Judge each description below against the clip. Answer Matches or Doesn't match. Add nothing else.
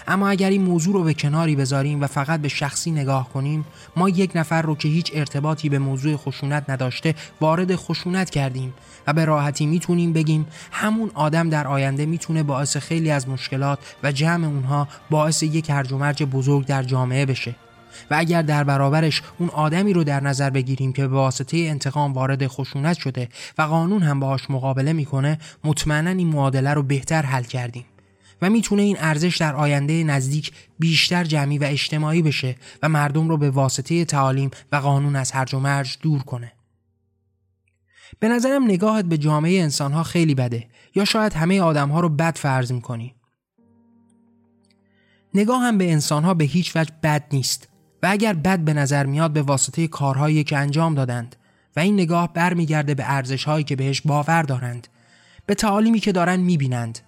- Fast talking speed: Matches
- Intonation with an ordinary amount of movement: Matches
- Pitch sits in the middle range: Matches